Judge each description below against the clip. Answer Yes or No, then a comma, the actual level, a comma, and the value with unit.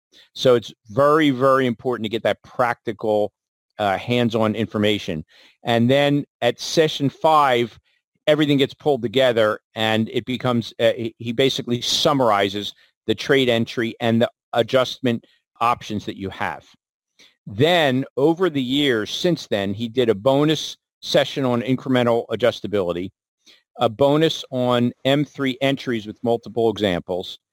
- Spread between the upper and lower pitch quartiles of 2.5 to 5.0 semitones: Yes, average, 3.6 semitones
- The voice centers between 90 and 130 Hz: Yes, low, 120 Hz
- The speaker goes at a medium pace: No, slow, 130 wpm